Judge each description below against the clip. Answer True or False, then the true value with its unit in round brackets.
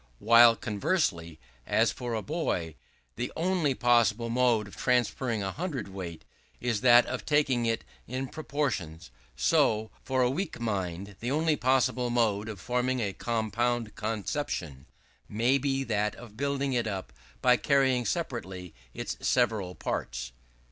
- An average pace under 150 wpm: True (140 wpm)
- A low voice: True (120 Hz)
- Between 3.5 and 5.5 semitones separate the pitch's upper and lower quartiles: True (4.2 semitones)